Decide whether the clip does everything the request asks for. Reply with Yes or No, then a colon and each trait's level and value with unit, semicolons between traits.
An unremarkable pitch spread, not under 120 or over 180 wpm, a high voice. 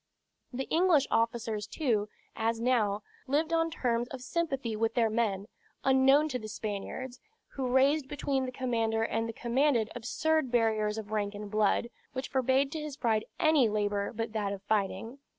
Yes: average, 3.7 semitones; average, 170 wpm; high, 235 Hz